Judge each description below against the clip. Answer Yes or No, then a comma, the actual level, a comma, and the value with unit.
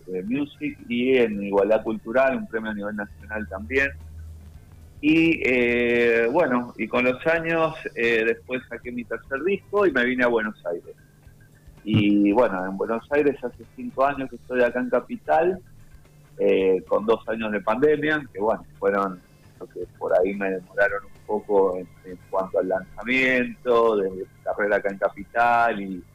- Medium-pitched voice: No, low, 120 Hz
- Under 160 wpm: No, average, 170 wpm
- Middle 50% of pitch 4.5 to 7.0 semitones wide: Yes, average, 5.2 semitones